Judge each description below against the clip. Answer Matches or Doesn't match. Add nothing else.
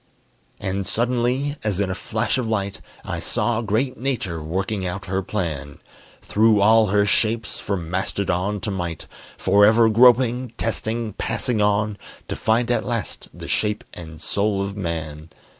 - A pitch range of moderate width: Matches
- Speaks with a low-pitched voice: Matches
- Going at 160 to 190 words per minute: Doesn't match